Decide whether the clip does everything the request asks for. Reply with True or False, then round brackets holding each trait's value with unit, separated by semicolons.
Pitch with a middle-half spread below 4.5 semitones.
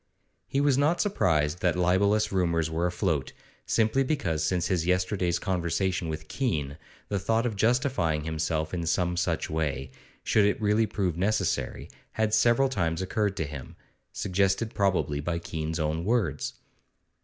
False (4.9 semitones)